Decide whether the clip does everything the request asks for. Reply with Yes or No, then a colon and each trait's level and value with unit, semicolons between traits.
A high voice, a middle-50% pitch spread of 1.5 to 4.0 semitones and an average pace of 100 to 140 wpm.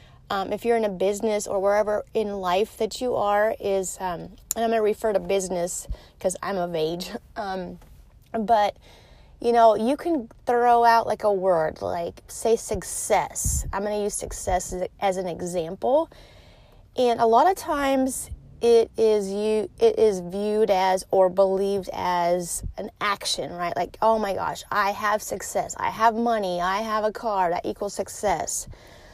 No: high, 210 Hz; average, 3.2 semitones; average, 175 wpm